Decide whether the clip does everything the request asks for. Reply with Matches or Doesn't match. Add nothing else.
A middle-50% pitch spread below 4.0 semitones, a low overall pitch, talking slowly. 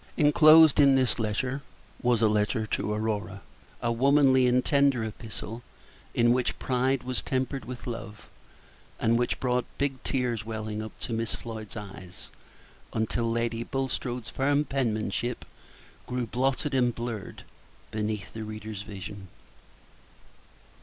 Matches